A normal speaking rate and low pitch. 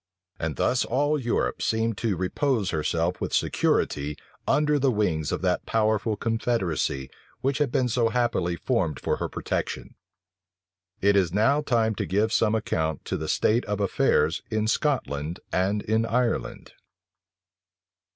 Yes: average, 145 wpm; low, 110 Hz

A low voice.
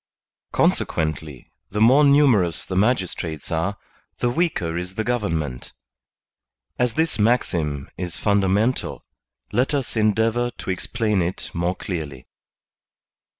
Yes: low, 100 Hz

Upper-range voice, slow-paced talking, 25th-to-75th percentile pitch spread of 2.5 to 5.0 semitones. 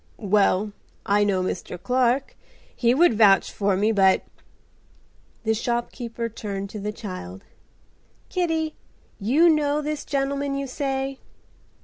No: high, 235 Hz; slow, 120 wpm; wide, 5.5 semitones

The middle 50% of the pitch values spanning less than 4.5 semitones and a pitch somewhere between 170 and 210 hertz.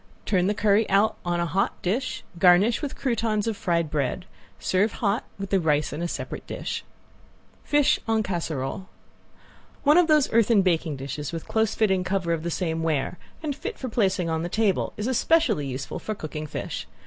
No: average, 5.0 semitones; high, 190 Hz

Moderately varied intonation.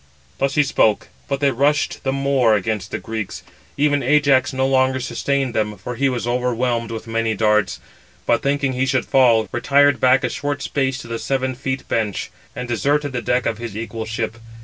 Yes: average, 3.2 semitones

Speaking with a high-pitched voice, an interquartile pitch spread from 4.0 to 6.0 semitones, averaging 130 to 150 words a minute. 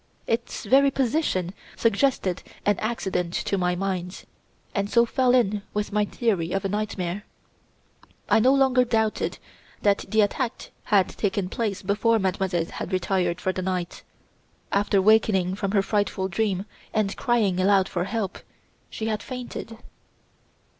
No: high, 200 Hz; average, 3.2 semitones; average, 145 wpm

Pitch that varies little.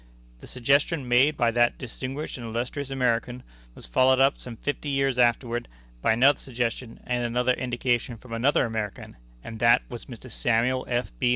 Yes: narrow, 1.9 semitones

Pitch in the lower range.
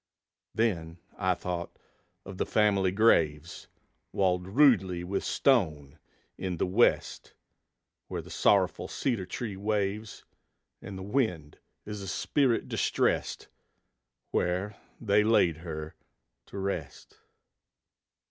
Yes: very low, 95 Hz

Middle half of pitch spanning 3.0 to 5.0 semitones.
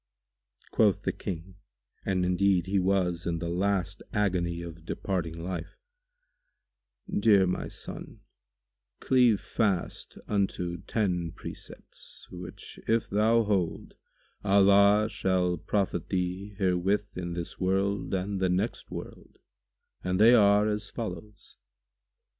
No: narrow, 2.4 semitones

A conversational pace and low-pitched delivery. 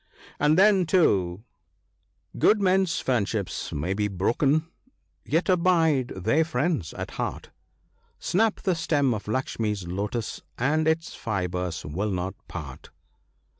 No: slow, 130 wpm; low, 125 Hz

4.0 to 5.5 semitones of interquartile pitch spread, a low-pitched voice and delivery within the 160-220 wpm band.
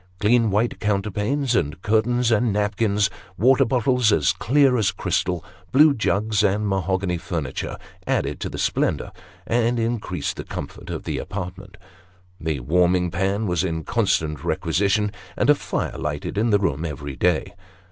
No: average, 4.4 semitones; low, 100 Hz; average, 150 wpm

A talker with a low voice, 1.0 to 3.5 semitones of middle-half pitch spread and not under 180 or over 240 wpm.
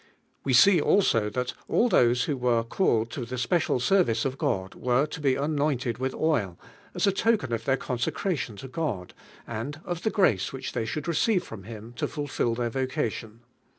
No: low, 130 Hz; average, 4.9 semitones; average, 190 wpm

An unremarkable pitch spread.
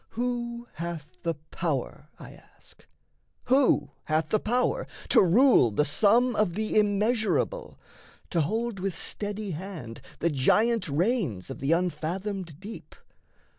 No: wide, 6.2 semitones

